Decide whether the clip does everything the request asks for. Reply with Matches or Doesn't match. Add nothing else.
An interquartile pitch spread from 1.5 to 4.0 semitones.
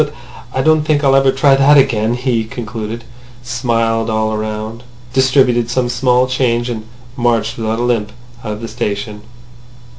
Matches